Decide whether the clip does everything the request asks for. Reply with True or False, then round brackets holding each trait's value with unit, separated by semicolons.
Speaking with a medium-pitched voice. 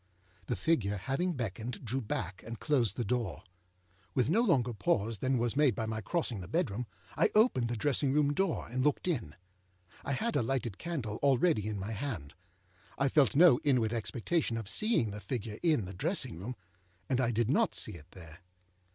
False (120 Hz)